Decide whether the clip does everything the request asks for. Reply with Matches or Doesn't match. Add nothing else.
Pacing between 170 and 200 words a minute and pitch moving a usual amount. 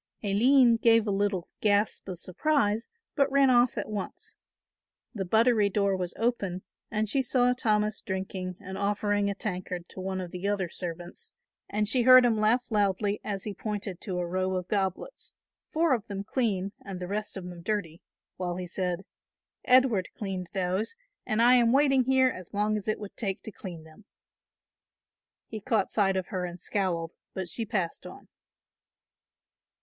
Matches